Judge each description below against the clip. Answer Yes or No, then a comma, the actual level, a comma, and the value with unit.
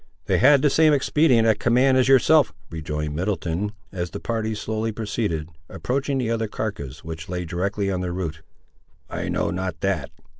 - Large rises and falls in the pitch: Yes, wide, 5.8 semitones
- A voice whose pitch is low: Yes, low, 105 Hz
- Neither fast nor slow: Yes, average, 175 wpm